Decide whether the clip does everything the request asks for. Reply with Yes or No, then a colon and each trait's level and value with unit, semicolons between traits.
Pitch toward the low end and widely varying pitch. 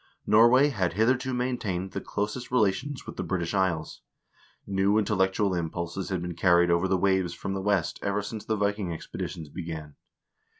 No: very low, 95 Hz; average, 3.5 semitones